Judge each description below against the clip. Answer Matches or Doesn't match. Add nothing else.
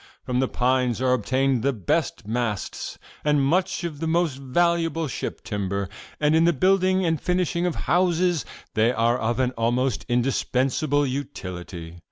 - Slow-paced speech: Doesn't match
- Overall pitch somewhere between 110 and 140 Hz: Matches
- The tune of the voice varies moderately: Doesn't match